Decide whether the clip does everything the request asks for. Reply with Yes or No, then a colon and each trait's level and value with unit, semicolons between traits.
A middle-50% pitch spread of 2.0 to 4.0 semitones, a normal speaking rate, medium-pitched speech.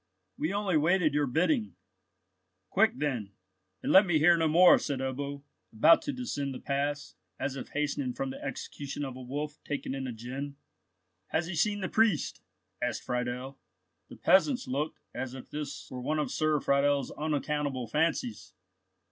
Yes: average, 3.2 semitones; average, 165 wpm; medium, 145 Hz